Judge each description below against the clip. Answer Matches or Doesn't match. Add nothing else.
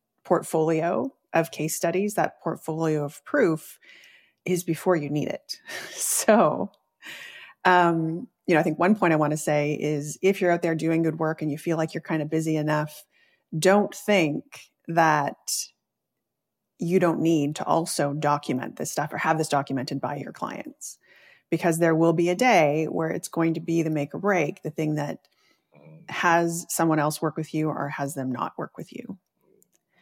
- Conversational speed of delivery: Matches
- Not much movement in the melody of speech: Matches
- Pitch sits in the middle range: Matches